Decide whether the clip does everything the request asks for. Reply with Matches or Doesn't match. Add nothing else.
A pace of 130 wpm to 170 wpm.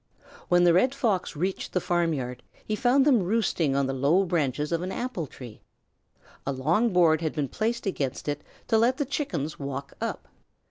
Doesn't match